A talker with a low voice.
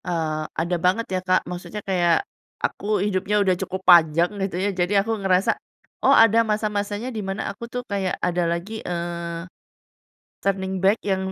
No: medium, 185 Hz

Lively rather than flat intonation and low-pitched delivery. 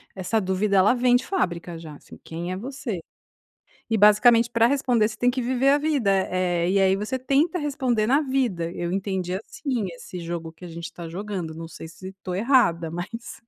No: wide, 6.0 semitones; high, 200 Hz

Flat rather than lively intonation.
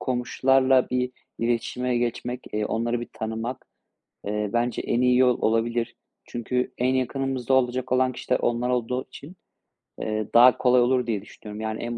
Yes: narrow, 1.6 semitones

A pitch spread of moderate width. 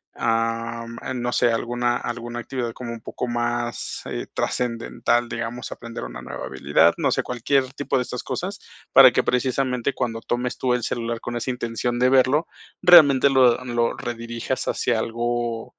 No: narrow, 1.5 semitones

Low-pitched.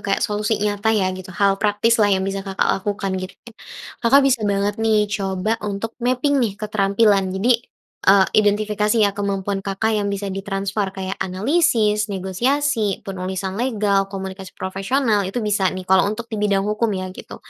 No: high, 205 Hz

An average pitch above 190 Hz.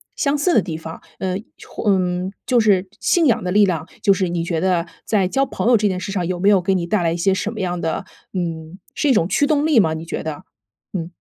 No: medium, 185 Hz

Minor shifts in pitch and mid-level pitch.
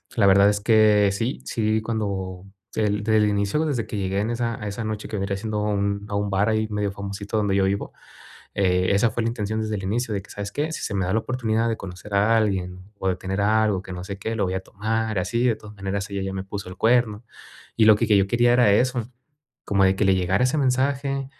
No: narrow, 2.3 semitones; low, 105 Hz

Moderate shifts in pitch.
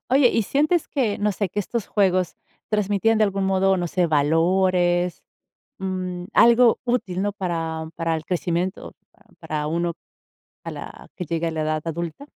Yes: average, 3.6 semitones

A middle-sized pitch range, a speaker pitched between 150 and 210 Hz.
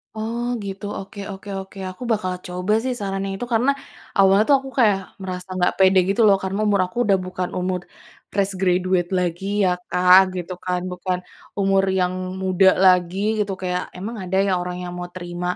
No: narrow, 1.6 semitones; high, 190 Hz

